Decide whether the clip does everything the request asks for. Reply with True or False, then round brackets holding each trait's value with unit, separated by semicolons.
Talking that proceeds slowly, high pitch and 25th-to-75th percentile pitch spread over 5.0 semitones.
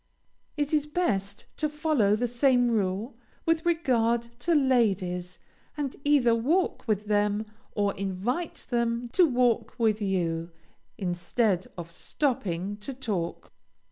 True (125 wpm; 230 Hz; 5.6 semitones)